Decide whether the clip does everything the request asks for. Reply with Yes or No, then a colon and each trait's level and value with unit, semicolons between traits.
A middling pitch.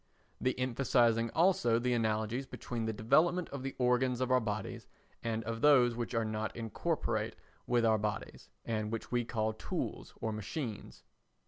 No: low, 115 Hz